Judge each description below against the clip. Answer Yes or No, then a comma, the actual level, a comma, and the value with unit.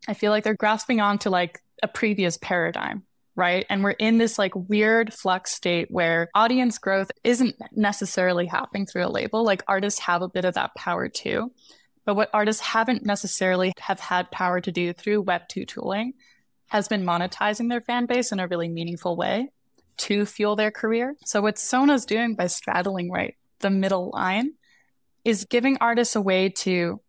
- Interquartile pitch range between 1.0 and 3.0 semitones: No, average, 3.5 semitones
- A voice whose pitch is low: No, high, 205 Hz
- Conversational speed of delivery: Yes, average, 180 wpm